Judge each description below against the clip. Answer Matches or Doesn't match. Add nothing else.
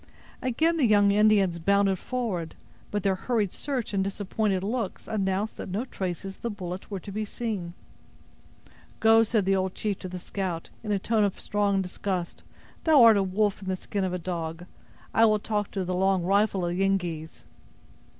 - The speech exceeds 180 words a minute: Matches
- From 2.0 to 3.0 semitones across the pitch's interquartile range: Matches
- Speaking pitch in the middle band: Doesn't match